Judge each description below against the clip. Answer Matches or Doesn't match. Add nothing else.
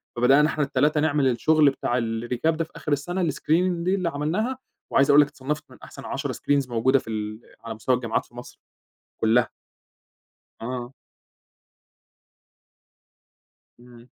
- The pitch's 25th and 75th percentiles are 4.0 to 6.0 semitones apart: Matches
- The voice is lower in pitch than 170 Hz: Matches